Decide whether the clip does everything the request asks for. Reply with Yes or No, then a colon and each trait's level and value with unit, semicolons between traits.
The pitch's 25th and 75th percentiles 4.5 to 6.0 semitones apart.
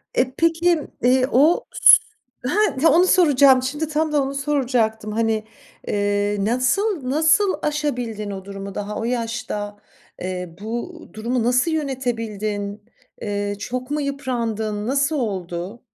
Yes: wide, 5.4 semitones